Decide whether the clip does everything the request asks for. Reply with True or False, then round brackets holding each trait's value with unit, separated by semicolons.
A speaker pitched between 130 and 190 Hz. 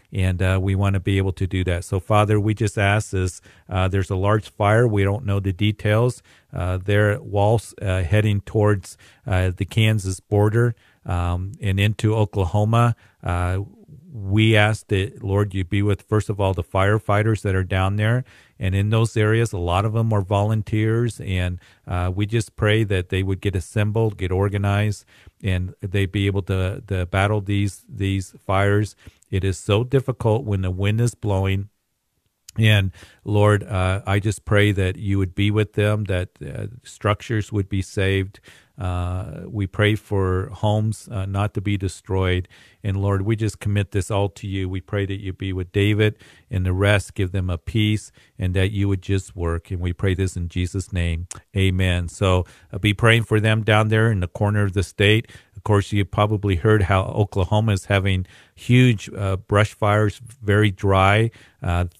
False (100 Hz)